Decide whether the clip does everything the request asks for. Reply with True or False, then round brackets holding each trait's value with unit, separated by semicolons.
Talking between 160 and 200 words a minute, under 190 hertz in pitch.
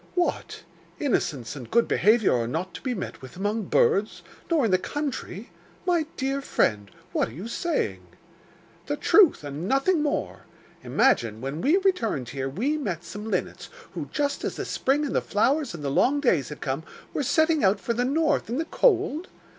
False (185 wpm; 235 Hz)